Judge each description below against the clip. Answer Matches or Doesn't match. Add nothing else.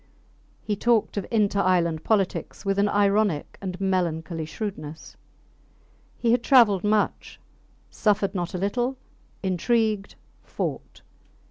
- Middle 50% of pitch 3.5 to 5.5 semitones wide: Doesn't match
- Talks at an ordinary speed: Doesn't match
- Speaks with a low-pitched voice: Doesn't match